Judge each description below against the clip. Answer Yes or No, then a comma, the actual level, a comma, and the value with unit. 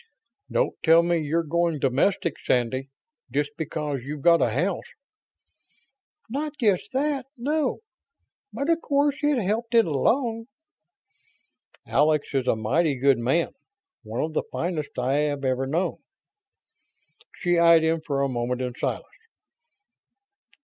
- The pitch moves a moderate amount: No, wide, 7.3 semitones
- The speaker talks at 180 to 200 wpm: No, slow, 135 wpm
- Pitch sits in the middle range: Yes, medium, 160 Hz